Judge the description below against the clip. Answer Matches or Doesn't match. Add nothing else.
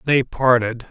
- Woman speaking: Doesn't match